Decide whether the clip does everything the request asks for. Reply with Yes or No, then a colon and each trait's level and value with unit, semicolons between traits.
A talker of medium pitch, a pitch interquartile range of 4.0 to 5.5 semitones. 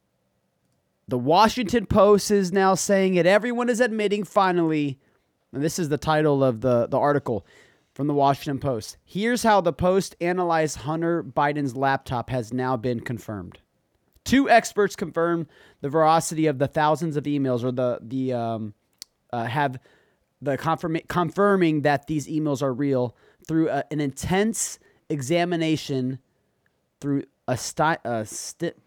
Yes: medium, 150 Hz; average, 5.1 semitones